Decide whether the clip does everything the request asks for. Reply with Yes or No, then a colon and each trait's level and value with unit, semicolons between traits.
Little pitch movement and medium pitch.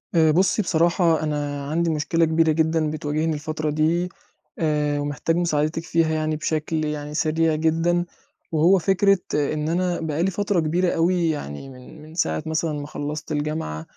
Yes: narrow, 1.8 semitones; medium, 155 Hz